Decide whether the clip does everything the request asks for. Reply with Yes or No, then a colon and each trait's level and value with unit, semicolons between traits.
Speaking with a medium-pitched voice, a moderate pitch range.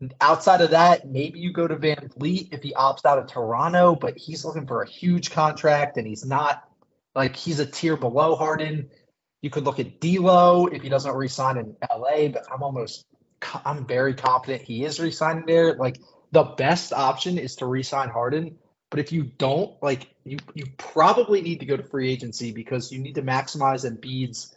Yes: medium, 145 Hz; average, 3.6 semitones